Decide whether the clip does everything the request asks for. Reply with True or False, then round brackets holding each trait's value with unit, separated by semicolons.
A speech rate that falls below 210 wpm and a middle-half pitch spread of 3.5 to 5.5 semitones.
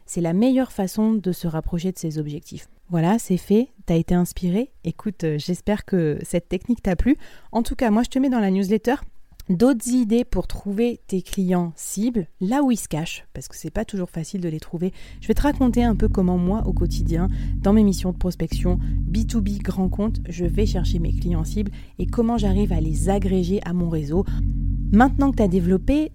False (215 wpm; 4.7 semitones)